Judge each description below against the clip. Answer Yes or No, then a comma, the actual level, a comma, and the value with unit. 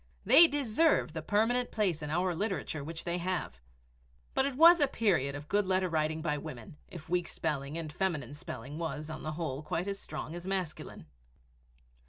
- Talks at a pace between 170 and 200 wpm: Yes, average, 185 wpm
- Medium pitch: Yes, medium, 170 Hz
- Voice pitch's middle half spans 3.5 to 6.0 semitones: Yes, average, 4.5 semitones